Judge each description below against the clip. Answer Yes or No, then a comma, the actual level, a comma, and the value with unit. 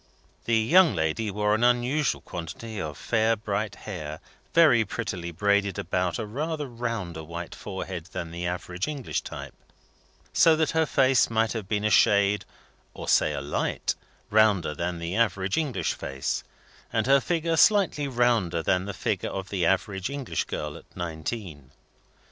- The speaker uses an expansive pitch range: Yes, wide, 5.7 semitones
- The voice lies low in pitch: Yes, low, 105 Hz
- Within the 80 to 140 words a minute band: No, average, 160 wpm